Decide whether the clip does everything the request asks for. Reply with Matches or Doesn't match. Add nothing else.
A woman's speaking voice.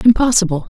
Doesn't match